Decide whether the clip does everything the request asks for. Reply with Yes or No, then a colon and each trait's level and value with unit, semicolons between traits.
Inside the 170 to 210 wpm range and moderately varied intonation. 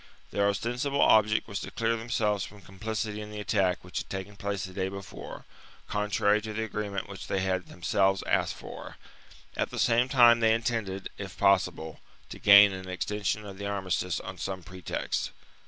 No: average, 180 wpm; narrow, 2.1 semitones